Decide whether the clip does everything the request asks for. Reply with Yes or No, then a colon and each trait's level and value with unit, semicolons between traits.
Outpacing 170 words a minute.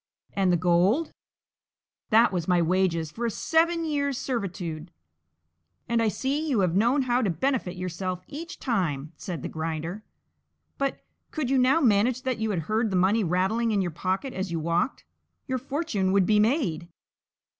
No: average, 165 wpm